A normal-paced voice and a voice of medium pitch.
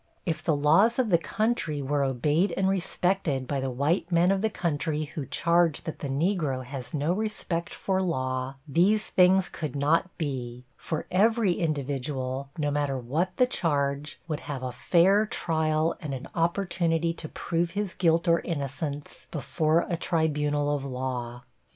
Yes: average, 165 wpm; medium, 155 Hz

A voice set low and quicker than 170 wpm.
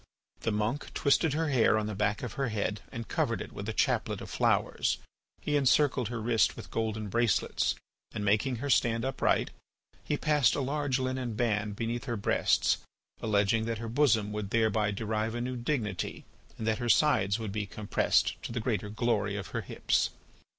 Yes: low, 115 Hz; average, 185 wpm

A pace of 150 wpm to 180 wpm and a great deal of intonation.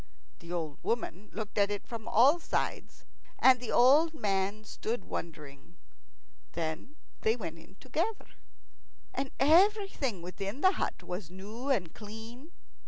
No: slow, 135 wpm; wide, 6.6 semitones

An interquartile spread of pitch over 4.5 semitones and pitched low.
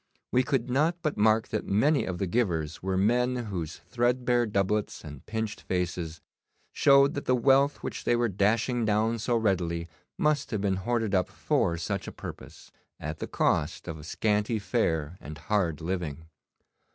Yes: wide, 5.6 semitones; low, 105 Hz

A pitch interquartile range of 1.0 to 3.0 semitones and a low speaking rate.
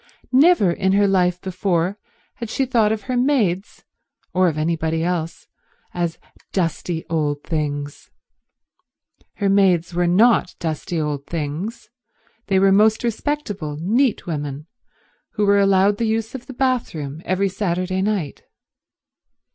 No: average, 4.5 semitones; slow, 130 wpm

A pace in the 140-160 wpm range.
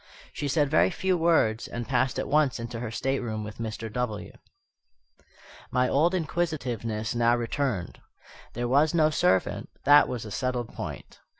Yes: average, 155 wpm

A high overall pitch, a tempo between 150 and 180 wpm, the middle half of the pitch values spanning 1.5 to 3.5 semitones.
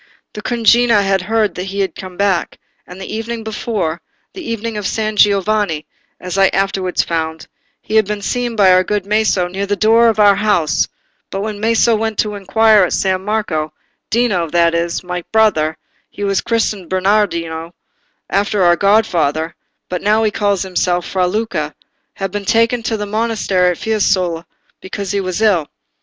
Yes: high, 200 Hz; average, 165 wpm; average, 3.2 semitones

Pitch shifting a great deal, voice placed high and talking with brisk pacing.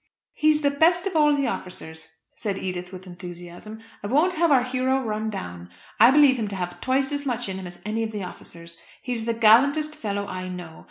Yes: wide, 7.2 semitones; high, 220 Hz; fast, 215 wpm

